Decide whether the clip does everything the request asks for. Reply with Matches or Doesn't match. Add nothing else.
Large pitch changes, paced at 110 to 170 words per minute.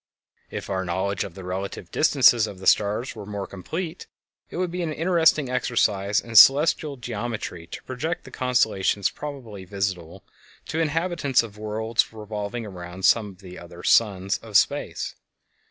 Matches